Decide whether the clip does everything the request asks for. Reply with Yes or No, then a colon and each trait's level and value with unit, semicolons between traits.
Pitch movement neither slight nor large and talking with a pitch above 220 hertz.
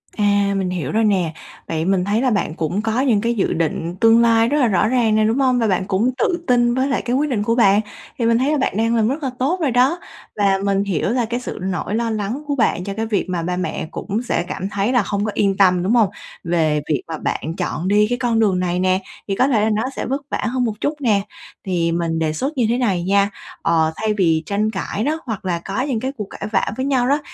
No: average, 4.5 semitones; high, 210 Hz